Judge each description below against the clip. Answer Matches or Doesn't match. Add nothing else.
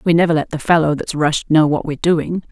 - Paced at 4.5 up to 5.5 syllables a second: Doesn't match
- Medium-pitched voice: Matches